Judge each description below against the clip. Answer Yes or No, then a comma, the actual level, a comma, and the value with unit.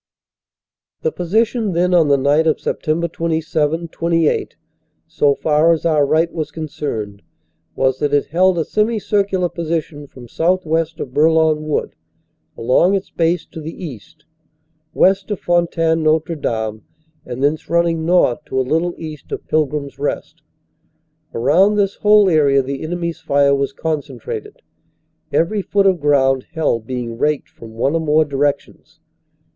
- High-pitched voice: No, medium, 160 Hz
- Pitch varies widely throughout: No, average, 3.2 semitones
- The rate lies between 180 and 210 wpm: No, average, 150 wpm